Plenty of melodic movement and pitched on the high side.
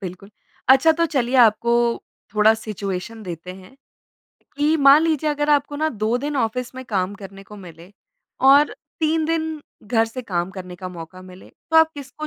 Yes: wide, 7.2 semitones; high, 235 Hz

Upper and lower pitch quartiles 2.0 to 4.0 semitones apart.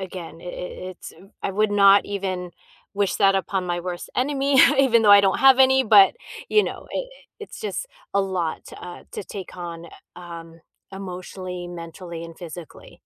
Yes: average, 2.8 semitones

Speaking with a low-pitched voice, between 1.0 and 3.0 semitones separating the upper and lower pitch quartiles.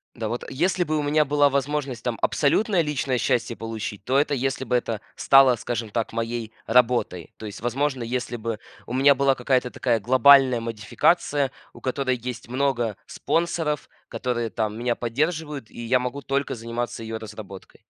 No: low, 125 Hz; average, 3.4 semitones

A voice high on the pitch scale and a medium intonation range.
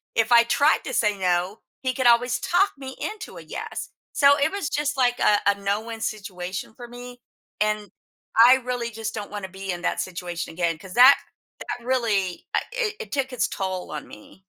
Yes: high, 225 Hz; average, 4.9 semitones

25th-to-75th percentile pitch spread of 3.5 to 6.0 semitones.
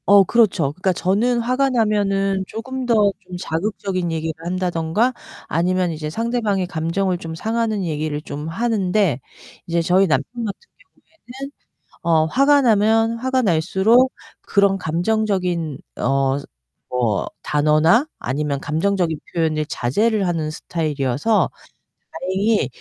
Yes: wide, 5.4 semitones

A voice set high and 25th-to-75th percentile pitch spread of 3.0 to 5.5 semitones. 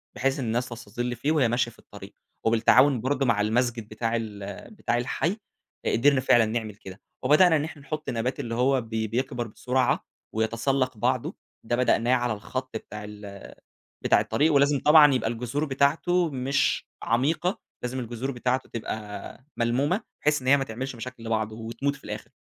No: low, 125 Hz; average, 3.4 semitones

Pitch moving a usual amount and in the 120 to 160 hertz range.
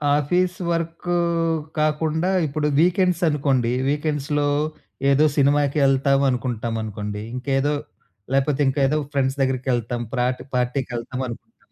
Yes: average, 3.2 semitones; medium, 140 Hz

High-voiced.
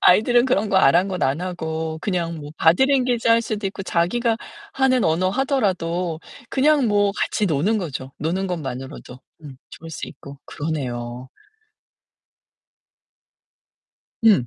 No: medium, 180 Hz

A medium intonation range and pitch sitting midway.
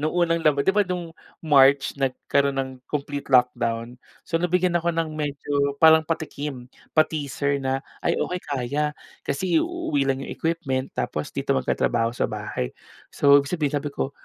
Yes: average, 3.2 semitones; medium, 145 Hz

